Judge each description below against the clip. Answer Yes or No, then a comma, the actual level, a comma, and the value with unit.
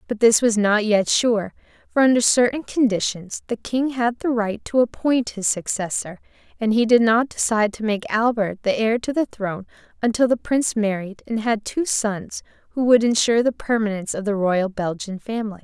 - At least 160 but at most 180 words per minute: No, average, 190 wpm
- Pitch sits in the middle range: No, high, 220 Hz